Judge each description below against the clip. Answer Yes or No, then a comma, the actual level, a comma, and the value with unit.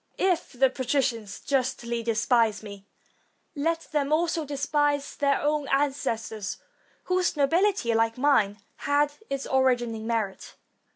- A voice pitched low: No, very high, 270 Hz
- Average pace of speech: No, slow, 120 wpm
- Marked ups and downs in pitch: No, average, 4.2 semitones